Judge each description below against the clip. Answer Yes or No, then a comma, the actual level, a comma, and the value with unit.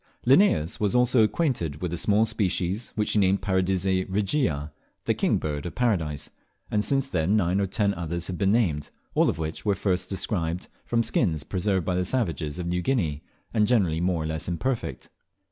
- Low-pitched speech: Yes, very low, 95 Hz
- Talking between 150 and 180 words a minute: No, average, 190 wpm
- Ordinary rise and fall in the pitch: Yes, average, 4.2 semitones